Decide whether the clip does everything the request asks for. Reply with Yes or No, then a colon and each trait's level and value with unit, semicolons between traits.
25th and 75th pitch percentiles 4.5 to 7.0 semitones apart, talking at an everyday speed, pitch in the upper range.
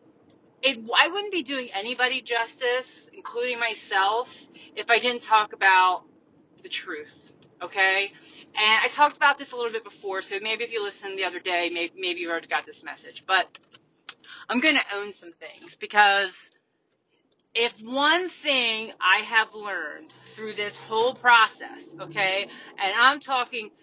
Yes: average, 4.9 semitones; average, 160 wpm; high, 220 Hz